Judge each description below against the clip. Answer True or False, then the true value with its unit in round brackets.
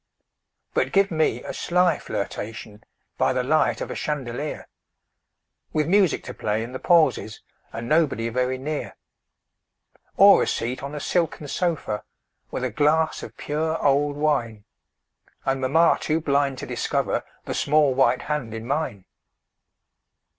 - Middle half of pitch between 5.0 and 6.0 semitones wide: False (4.1 semitones)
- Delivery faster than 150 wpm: False (145 wpm)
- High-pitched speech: False (140 Hz)